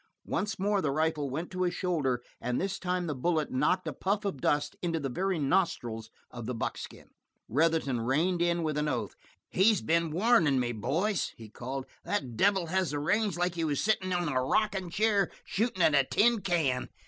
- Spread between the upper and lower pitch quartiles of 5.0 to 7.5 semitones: Yes, wide, 5.6 semitones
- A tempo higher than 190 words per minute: Yes, average, 200 wpm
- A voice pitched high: No, medium, 165 Hz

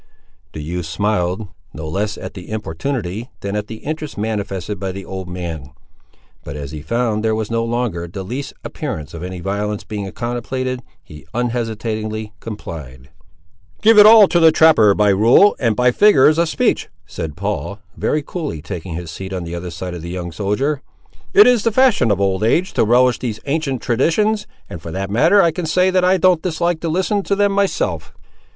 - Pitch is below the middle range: Yes, low, 110 Hz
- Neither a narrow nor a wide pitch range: No, wide, 8.9 semitones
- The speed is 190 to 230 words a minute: Yes, average, 195 wpm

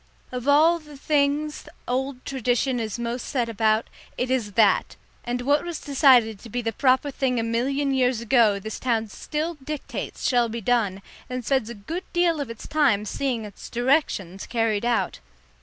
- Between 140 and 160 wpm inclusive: No, average, 175 wpm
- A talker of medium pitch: No, high, 245 Hz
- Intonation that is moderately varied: Yes, average, 3.7 semitones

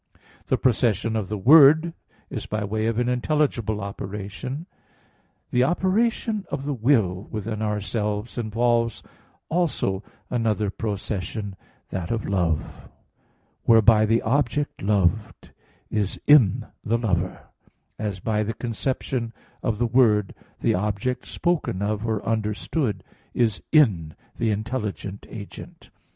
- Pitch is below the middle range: Yes, low, 110 Hz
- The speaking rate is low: Yes, slow, 120 wpm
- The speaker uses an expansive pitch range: No, average, 3.4 semitones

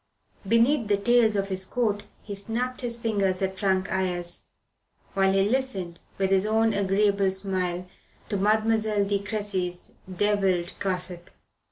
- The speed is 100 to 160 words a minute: Yes, average, 140 wpm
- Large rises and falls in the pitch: No, narrow, 2.5 semitones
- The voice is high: Yes, high, 200 Hz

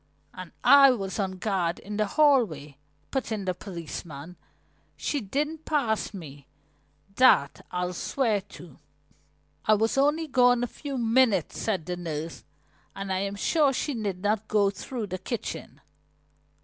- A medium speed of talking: Yes, average, 150 wpm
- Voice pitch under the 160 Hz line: No, high, 205 Hz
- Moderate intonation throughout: No, wide, 5.9 semitones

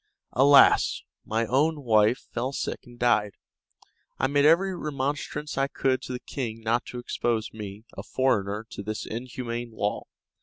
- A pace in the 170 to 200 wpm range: No, average, 155 wpm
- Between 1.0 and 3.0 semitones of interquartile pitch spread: No, average, 3.7 semitones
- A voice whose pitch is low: Yes, low, 120 Hz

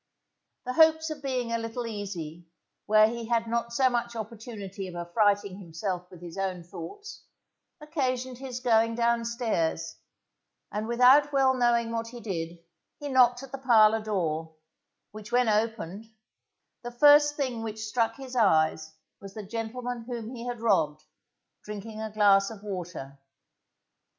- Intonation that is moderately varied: Yes, average, 3.9 semitones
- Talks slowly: No, average, 150 wpm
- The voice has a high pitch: Yes, high, 225 Hz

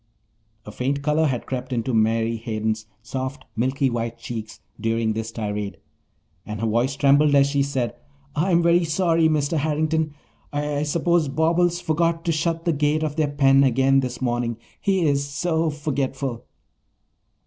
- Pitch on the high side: No, medium, 140 Hz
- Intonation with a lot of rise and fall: No, average, 4.9 semitones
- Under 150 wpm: No, average, 155 wpm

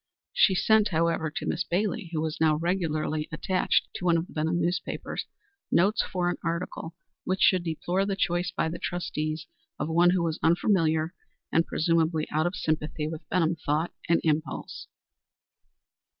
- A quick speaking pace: No, average, 165 wpm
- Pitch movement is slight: Yes, narrow, 2.1 semitones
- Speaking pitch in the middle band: Yes, medium, 165 Hz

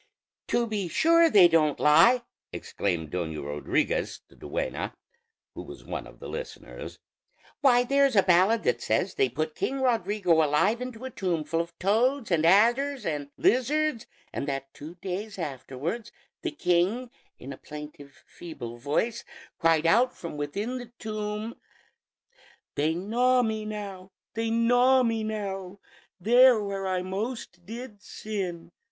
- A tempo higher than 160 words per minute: No, average, 145 wpm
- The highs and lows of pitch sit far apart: Yes, wide, 6.4 semitones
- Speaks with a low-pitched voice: No, high, 200 Hz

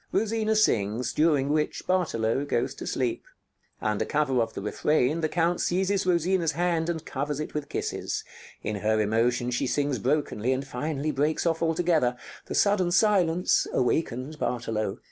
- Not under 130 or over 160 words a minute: Yes, average, 155 wpm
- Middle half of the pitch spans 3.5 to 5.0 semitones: No, wide, 5.6 semitones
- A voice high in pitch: No, medium, 150 Hz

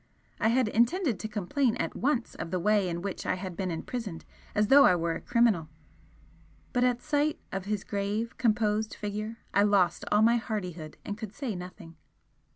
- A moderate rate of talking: Yes, average, 185 wpm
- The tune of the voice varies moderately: Yes, average, 4.3 semitones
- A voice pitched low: No, high, 210 Hz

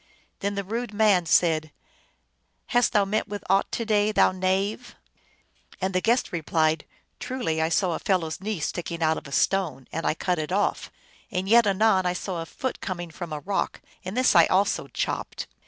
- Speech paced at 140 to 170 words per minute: No, fast, 205 wpm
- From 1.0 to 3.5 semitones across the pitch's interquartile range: No, average, 4.0 semitones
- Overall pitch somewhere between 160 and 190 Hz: Yes, medium, 185 Hz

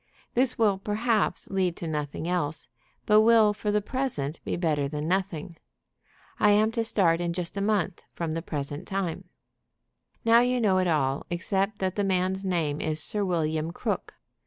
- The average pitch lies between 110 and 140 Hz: No, medium, 185 Hz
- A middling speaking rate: Yes, average, 175 wpm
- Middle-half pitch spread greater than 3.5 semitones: Yes, average, 4.5 semitones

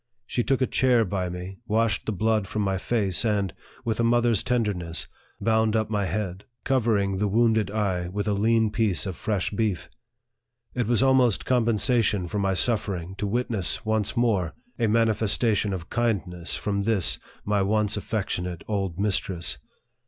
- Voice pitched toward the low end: Yes, low, 105 Hz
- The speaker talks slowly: No, average, 160 wpm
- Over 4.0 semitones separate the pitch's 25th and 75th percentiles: No, average, 2.8 semitones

